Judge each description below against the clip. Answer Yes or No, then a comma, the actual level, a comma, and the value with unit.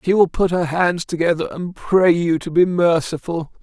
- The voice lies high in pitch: No, medium, 170 Hz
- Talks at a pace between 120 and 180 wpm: No, average, 200 wpm